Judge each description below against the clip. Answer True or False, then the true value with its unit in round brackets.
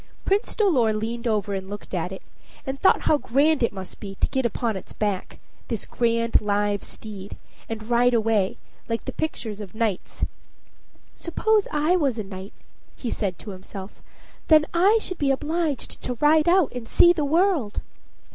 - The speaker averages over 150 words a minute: True (175 wpm)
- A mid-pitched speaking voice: False (230 Hz)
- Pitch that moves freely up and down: True (6.8 semitones)